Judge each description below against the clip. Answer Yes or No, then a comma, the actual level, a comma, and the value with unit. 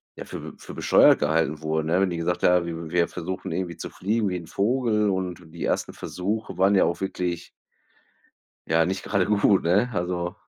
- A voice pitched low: Yes, very low, 90 Hz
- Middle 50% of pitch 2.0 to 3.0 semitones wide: Yes, narrow, 2.5 semitones